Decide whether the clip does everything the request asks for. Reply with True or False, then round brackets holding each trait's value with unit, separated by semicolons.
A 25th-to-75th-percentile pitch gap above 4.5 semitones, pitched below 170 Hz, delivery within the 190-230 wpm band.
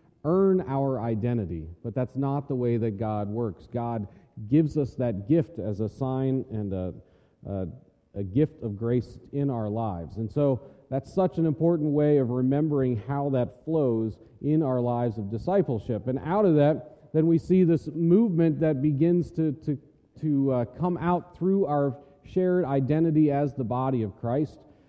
False (5.0 semitones; 135 Hz; 175 wpm)